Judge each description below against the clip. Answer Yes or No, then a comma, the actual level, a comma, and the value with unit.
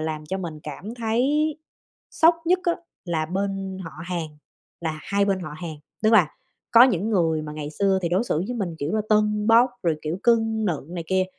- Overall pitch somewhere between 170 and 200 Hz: Yes, high, 190 Hz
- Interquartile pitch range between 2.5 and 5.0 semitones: No, wide, 5.5 semitones